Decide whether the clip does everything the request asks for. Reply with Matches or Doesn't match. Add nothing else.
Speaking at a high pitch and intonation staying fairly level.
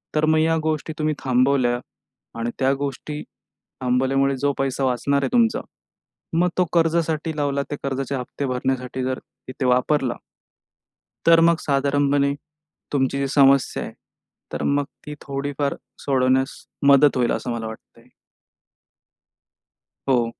Doesn't match